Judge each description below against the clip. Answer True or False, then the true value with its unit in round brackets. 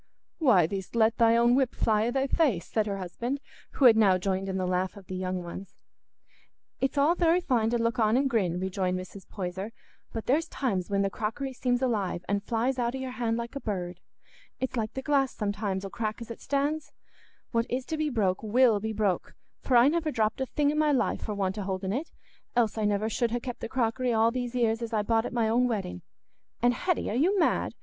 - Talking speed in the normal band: False (235 wpm)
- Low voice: False (230 Hz)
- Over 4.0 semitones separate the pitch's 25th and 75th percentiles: True (4.4 semitones)